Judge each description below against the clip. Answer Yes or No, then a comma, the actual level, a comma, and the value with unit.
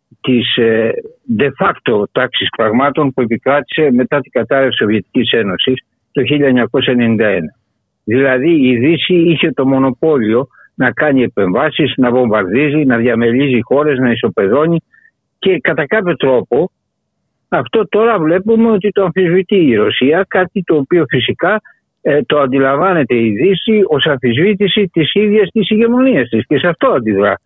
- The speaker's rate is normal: Yes, average, 140 wpm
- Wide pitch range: Yes, wide, 7.5 semitones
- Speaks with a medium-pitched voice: Yes, medium, 145 Hz